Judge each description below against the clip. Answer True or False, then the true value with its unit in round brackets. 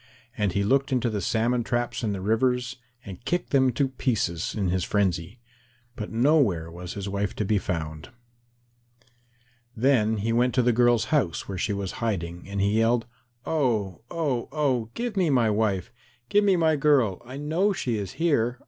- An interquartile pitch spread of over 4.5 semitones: True (4.9 semitones)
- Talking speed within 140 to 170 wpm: False (180 wpm)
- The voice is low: True (115 Hz)